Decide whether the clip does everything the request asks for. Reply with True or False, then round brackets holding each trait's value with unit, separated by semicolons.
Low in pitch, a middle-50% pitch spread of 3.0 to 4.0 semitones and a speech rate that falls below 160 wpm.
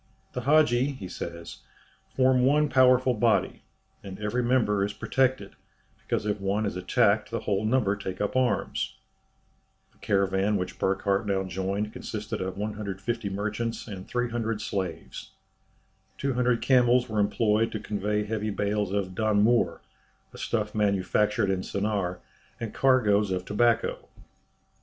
True (105 Hz; 3.3 semitones; 140 wpm)